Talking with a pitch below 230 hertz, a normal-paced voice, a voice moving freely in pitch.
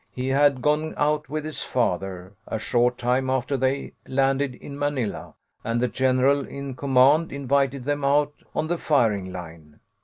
No: low, 135 Hz; average, 160 wpm; average, 2.7 semitones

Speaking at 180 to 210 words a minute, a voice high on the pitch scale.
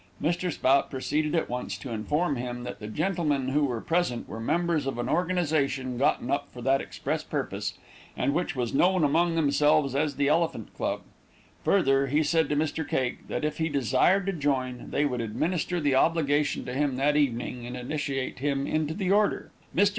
No: average, 190 wpm; medium, 145 Hz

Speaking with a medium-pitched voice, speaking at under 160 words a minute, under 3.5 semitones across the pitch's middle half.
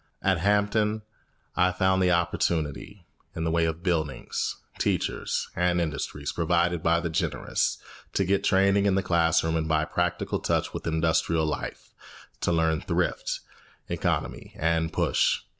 No: very low, 85 Hz; average, 140 wpm; narrow, 2.6 semitones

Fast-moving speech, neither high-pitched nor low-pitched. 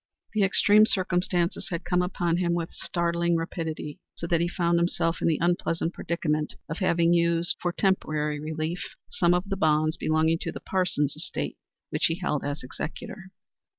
No: average, 170 wpm; medium, 170 Hz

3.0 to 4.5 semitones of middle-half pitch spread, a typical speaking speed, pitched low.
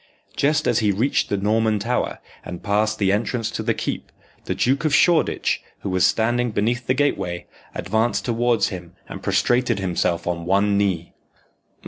Yes: average, 3.9 semitones; average, 165 wpm; low, 110 Hz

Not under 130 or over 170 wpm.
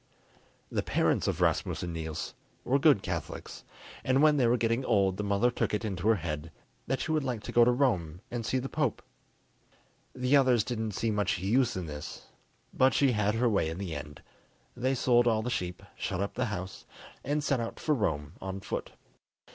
No: fast, 205 wpm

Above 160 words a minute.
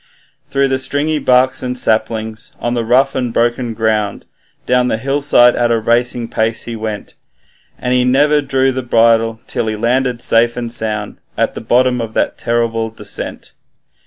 Yes: average, 170 wpm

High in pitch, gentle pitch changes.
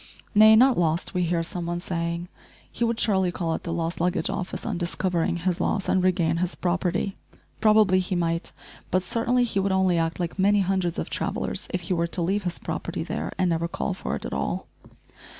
No: medium, 180 Hz; narrow, 2.3 semitones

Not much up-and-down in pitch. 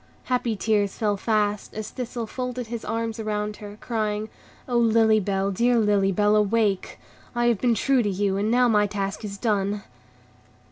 Yes: narrow, 2.2 semitones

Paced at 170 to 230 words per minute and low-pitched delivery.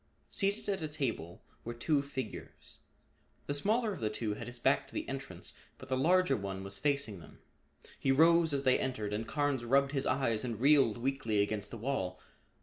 Yes: average, 195 wpm; low, 130 Hz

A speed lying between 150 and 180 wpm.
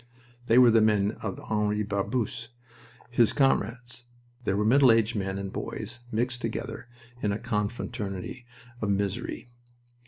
No: slow, 135 wpm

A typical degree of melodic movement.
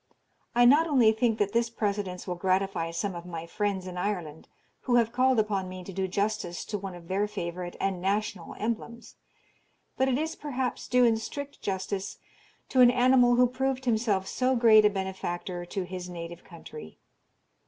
Yes: average, 4.9 semitones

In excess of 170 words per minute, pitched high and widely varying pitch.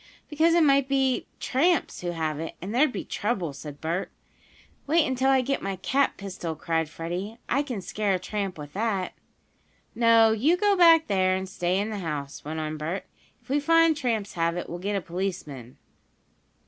Yes: average, 190 wpm; high, 200 Hz; wide, 7.8 semitones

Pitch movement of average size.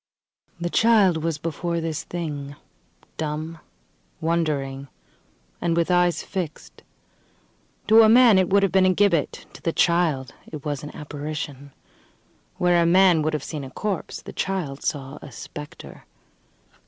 Yes: average, 3.3 semitones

